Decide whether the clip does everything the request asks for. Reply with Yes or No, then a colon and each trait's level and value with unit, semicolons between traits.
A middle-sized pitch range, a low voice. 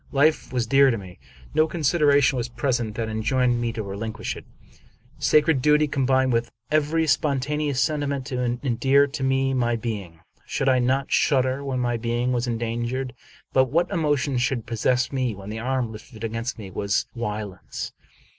Yes: average, 3.2 semitones; low, 130 Hz